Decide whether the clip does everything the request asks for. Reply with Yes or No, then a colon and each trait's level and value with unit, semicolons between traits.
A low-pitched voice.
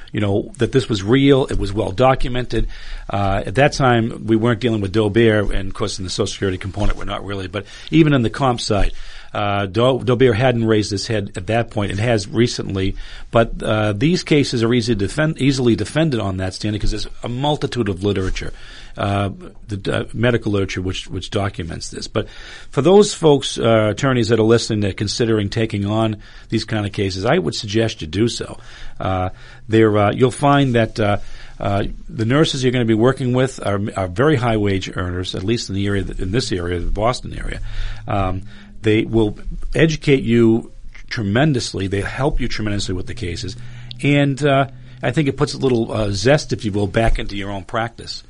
Yes: low, 110 Hz